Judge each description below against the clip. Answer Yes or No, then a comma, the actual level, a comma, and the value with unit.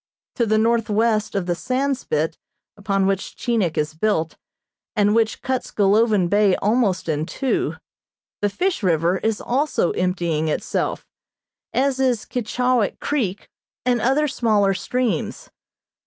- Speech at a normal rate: No, slow, 130 wpm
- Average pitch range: Yes, average, 5.0 semitones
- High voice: Yes, high, 215 Hz